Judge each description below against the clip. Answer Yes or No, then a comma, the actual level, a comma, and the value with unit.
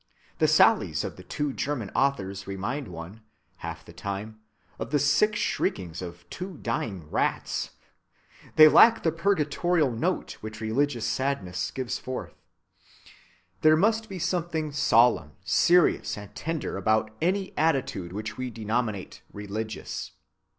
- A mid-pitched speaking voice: No, low, 125 Hz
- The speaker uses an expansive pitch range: Yes, wide, 7.2 semitones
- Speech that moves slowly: Yes, slow, 130 wpm